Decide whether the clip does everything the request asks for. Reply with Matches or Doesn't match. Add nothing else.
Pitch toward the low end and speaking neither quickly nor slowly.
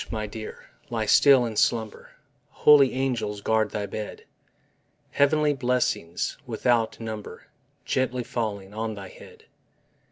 Doesn't match